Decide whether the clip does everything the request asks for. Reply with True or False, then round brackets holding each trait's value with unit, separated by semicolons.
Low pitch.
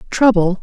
False (200 Hz)